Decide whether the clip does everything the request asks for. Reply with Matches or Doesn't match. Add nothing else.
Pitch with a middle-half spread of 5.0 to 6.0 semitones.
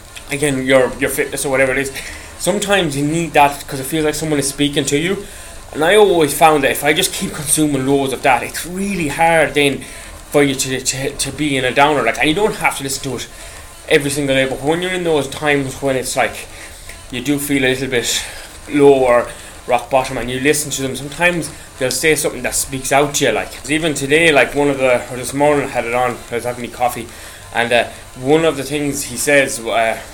Doesn't match